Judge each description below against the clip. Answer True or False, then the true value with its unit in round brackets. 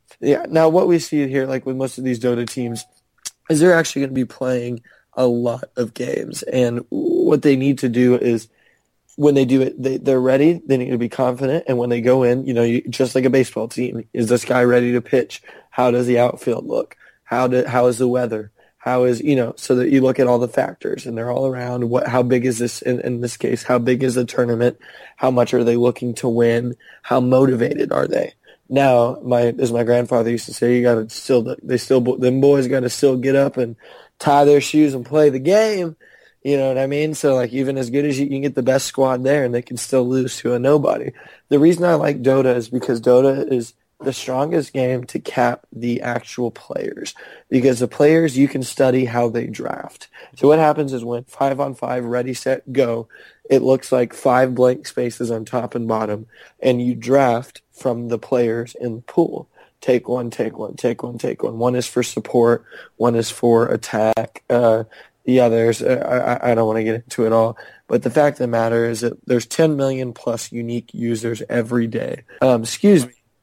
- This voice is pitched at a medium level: False (125 Hz)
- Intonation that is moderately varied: False (2.0 semitones)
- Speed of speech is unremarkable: False (220 wpm)